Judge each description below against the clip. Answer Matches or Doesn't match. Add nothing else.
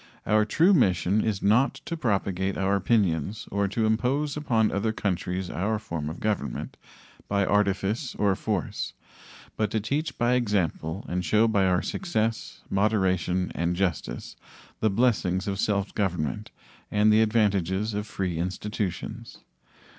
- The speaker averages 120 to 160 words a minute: Matches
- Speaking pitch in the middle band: Doesn't match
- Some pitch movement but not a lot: Matches